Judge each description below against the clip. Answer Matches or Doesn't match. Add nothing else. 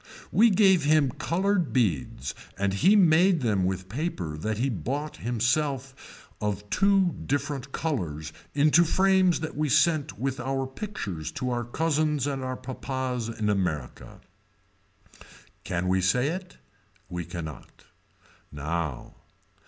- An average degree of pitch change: Doesn't match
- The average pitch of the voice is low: Matches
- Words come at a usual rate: Doesn't match